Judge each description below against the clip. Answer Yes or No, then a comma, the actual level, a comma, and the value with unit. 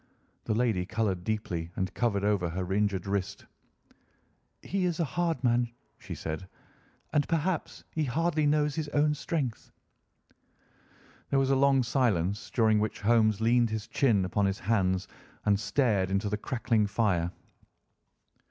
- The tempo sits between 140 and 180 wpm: Yes, average, 145 wpm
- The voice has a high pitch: No, low, 110 Hz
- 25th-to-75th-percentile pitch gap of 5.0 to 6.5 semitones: Yes, wide, 5.6 semitones